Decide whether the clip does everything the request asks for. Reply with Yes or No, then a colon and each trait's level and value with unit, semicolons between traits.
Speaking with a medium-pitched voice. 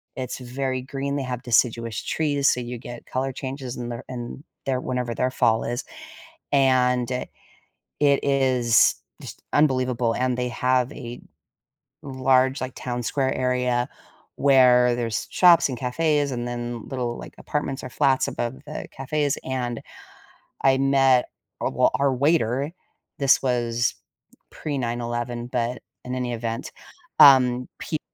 No: low, 125 Hz